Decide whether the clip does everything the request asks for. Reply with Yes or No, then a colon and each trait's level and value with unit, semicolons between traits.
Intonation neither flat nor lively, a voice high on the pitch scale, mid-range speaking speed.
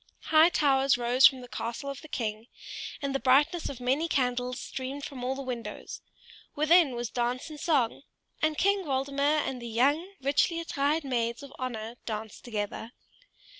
Yes: average, 3.4 semitones; very high, 265 Hz; average, 170 wpm